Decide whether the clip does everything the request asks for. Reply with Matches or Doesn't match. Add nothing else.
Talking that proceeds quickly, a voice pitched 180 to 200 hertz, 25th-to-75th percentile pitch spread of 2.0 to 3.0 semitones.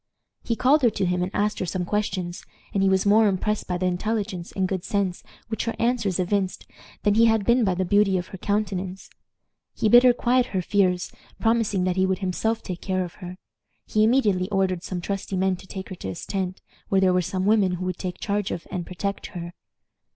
Matches